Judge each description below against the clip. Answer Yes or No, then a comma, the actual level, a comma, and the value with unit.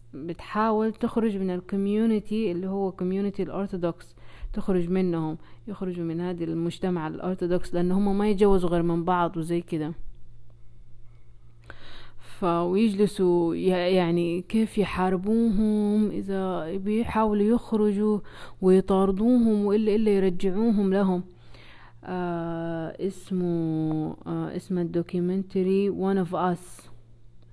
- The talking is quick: No, average, 95 wpm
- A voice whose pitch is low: No, medium, 185 Hz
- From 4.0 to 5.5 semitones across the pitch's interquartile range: No, average, 3.3 semitones